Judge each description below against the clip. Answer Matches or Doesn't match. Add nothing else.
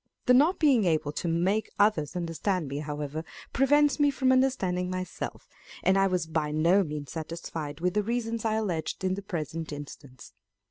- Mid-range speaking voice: Matches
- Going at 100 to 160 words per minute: Doesn't match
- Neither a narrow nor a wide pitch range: Doesn't match